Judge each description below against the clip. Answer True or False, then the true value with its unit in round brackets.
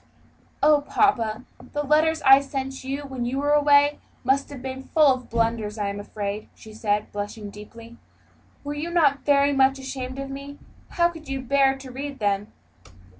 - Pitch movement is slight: False (3.8 semitones)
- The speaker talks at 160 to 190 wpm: True (175 wpm)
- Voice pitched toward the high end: True (270 Hz)